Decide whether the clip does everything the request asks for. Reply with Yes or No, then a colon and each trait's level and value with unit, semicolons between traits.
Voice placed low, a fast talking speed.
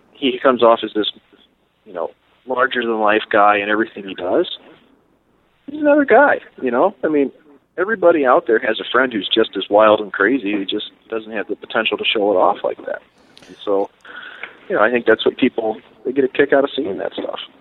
Yes: low, 125 Hz; fast, 220 wpm